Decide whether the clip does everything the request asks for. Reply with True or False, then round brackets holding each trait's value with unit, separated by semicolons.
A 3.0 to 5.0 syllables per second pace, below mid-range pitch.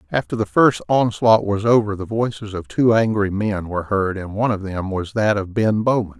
False (5.3 syllables/s; 105 Hz)